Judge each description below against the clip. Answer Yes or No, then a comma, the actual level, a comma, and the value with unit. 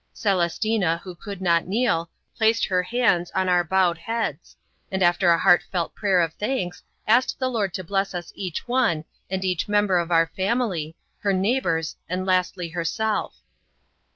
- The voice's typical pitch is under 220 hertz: Yes, medium, 185 Hz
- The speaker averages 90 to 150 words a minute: No, average, 160 wpm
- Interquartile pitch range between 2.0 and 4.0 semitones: Yes, average, 3.3 semitones